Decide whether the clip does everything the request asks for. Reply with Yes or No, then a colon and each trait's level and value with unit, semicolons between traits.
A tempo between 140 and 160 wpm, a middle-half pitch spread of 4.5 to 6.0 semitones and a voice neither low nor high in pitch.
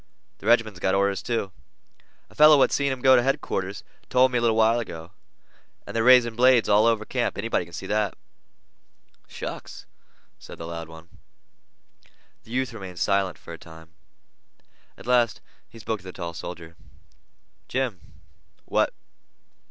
No: average, 155 wpm; average, 4.9 semitones; low, 110 Hz